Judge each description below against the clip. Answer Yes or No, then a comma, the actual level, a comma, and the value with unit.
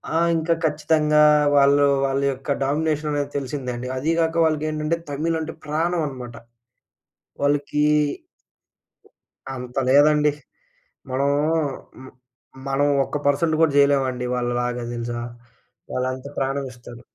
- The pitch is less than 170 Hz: Yes, medium, 140 Hz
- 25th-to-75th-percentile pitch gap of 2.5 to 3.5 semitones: Yes, average, 2.8 semitones